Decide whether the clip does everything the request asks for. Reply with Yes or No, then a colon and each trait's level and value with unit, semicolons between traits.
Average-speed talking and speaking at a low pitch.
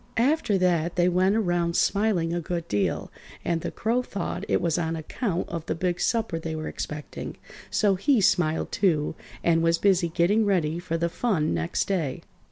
No: average, 180 wpm; medium, 175 Hz